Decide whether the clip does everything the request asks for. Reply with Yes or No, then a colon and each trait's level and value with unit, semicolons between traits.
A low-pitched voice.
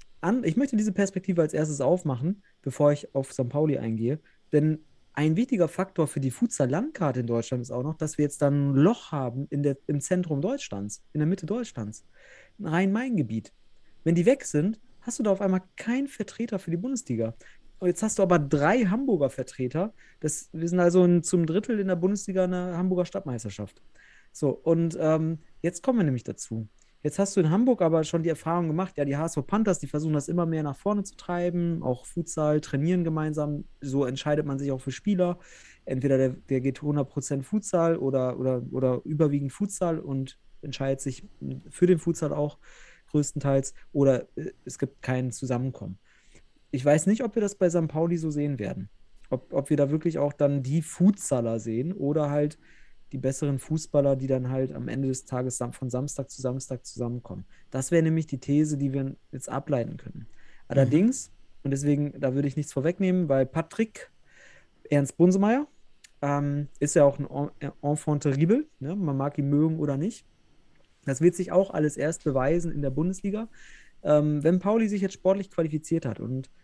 No: medium, 150 Hz